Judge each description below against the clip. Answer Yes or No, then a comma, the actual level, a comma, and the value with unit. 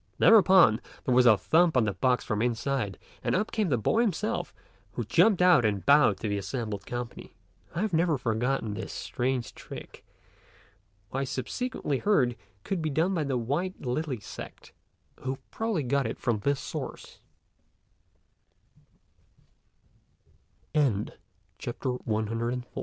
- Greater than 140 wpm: No, slow, 135 wpm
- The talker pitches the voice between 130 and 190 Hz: Yes, low, 135 Hz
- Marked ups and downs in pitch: Yes, wide, 6.7 semitones